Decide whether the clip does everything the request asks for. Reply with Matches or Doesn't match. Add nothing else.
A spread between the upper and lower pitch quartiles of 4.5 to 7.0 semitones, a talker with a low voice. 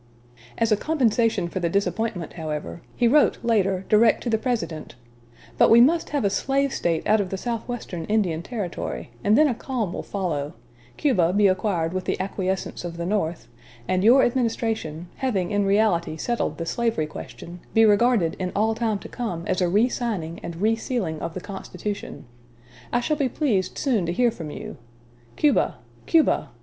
Doesn't match